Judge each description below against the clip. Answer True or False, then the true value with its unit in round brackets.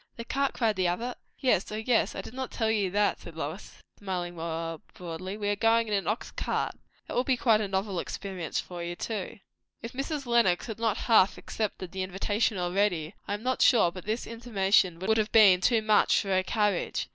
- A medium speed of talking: False (210 wpm)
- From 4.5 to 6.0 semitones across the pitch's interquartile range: False (3.7 semitones)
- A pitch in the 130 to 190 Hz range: False (205 Hz)